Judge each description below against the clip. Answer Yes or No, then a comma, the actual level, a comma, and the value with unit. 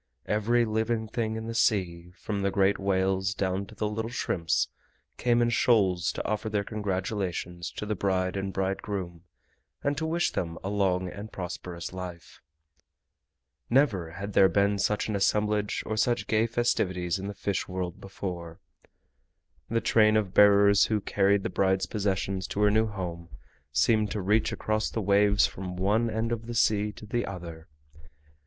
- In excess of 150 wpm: Yes, average, 170 wpm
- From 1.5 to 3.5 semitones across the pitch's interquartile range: Yes, narrow, 2.5 semitones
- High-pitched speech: No, low, 100 Hz